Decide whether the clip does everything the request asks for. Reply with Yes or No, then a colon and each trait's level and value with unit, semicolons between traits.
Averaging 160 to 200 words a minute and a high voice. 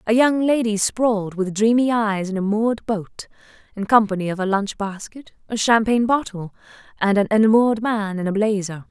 Yes: average, 180 wpm; high, 215 Hz